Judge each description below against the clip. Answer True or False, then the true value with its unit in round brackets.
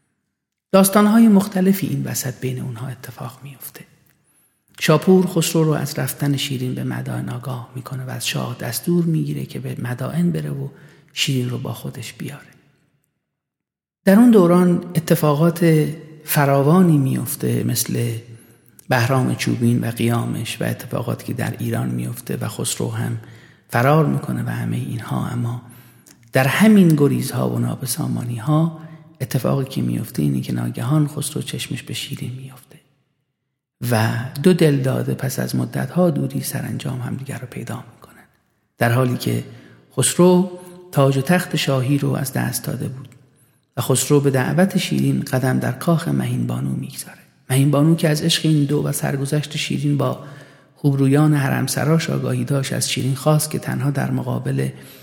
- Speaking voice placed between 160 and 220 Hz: False (135 Hz)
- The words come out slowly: False (150 wpm)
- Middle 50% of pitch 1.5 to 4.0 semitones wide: False (4.7 semitones)